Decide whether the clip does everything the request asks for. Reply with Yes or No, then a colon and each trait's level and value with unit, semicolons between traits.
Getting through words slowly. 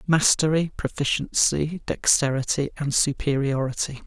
Yes: slow, 75 wpm